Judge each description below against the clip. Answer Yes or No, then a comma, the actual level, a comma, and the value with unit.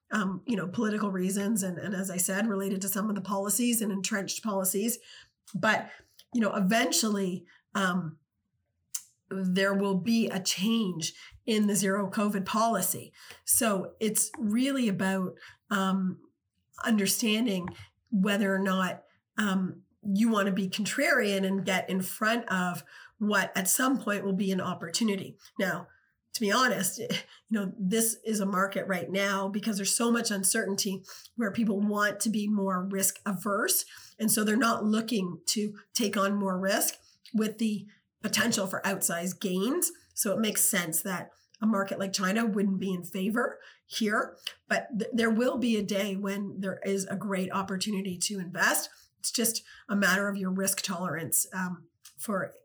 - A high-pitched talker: Yes, high, 200 Hz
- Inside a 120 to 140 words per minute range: No, average, 160 wpm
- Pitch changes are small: Yes, narrow, 2.2 semitones